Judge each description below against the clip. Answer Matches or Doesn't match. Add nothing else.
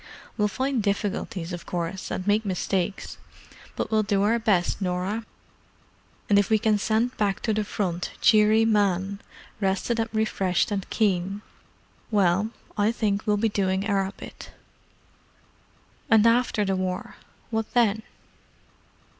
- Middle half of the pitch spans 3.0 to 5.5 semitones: Doesn't match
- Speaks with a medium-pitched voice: Doesn't match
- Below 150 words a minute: Matches